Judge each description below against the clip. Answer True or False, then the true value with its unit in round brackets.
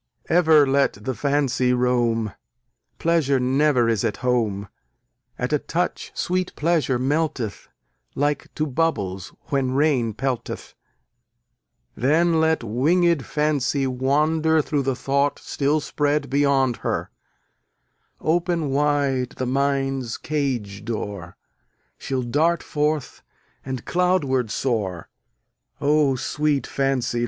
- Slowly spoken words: True (110 wpm)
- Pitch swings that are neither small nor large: True (3.4 semitones)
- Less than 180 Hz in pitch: True (135 Hz)